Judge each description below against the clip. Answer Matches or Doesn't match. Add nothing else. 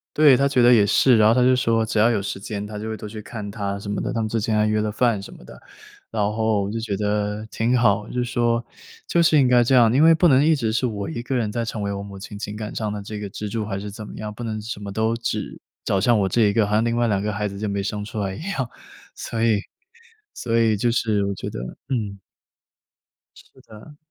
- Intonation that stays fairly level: Matches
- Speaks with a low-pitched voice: Matches